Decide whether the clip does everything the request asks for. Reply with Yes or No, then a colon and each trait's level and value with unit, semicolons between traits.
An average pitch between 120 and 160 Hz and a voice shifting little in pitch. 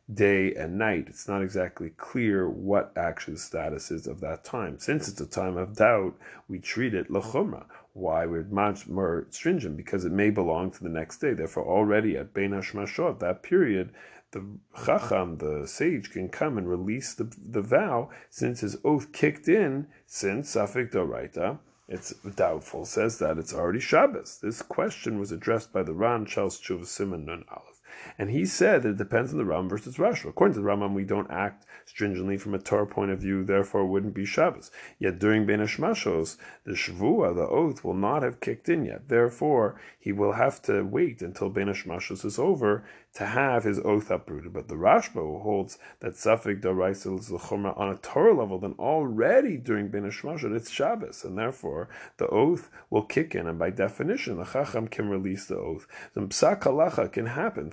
No: low, 100 Hz; narrow, 1.6 semitones